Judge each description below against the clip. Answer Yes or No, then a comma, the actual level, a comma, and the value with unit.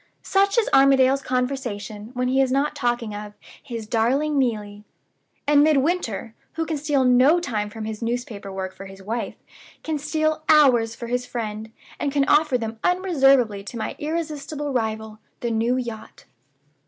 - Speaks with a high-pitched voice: Yes, very high, 250 Hz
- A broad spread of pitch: No, average, 4.8 semitones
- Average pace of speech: Yes, average, 160 wpm